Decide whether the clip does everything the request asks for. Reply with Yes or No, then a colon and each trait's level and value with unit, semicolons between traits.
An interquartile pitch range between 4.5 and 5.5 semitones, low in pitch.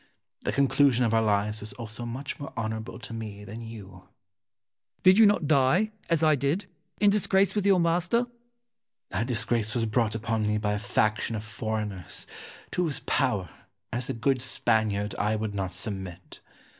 Yes: average, 5.0 semitones; low, 115 Hz